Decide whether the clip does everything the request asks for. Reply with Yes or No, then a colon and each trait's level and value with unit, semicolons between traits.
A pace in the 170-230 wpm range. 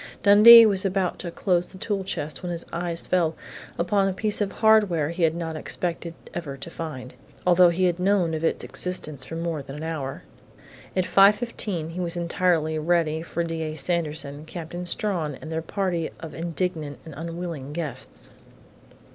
Yes: average, 175 wpm